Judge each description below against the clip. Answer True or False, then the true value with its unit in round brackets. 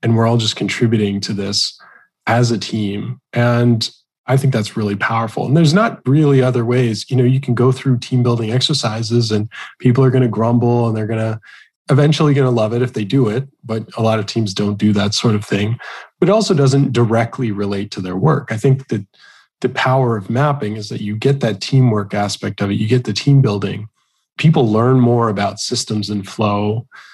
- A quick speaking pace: True (215 wpm)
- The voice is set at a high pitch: False (115 Hz)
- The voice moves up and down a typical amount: True (3.3 semitones)